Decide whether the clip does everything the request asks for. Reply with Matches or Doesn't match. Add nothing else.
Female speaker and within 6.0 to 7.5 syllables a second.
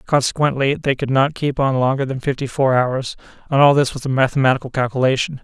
Doesn't match